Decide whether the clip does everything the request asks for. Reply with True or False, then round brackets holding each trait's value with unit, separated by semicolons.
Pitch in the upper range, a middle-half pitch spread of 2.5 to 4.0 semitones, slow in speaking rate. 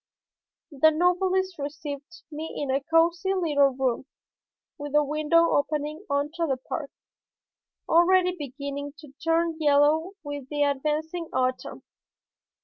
True (300 Hz; 2.9 semitones; 120 wpm)